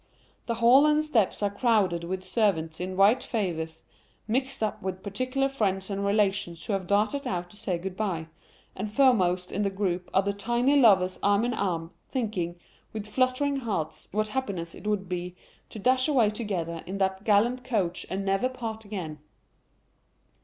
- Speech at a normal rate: Yes, average, 175 wpm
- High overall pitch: Yes, high, 200 Hz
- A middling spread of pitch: Yes, average, 4.2 semitones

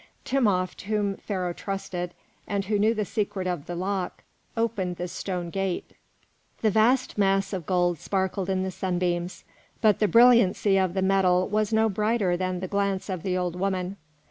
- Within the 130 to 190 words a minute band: Yes, average, 170 wpm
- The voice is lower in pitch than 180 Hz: No, high, 190 Hz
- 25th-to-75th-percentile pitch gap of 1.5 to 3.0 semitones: Yes, narrow, 2.4 semitones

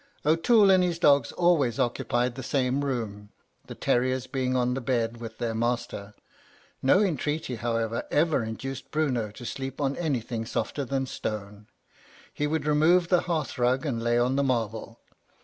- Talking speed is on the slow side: No, average, 165 wpm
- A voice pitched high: No, low, 130 Hz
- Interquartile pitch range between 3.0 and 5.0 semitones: Yes, average, 4.1 semitones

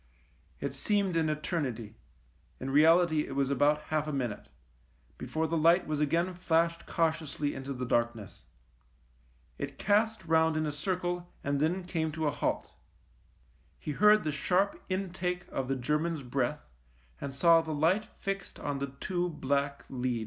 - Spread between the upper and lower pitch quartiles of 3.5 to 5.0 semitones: Yes, average, 3.9 semitones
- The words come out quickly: No, average, 165 wpm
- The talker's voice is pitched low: No, medium, 155 Hz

